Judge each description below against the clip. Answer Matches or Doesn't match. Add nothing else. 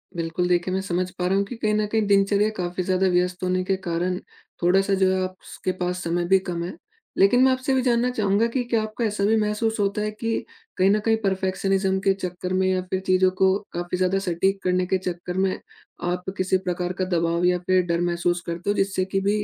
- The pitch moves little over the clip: Matches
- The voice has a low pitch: Doesn't match